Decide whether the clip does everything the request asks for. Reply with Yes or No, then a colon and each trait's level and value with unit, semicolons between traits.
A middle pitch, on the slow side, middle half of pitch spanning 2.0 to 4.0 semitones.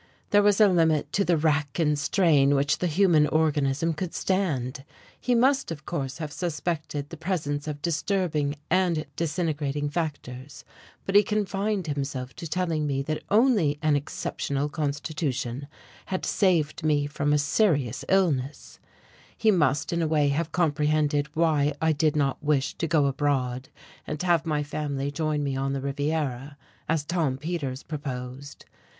No: medium, 150 Hz; average, 155 wpm; average, 3.0 semitones